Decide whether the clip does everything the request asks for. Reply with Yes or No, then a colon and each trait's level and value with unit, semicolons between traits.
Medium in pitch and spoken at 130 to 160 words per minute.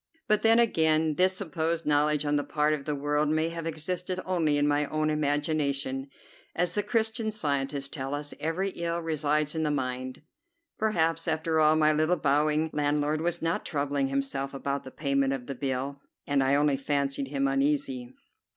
No: medium, 150 Hz; average, 180 wpm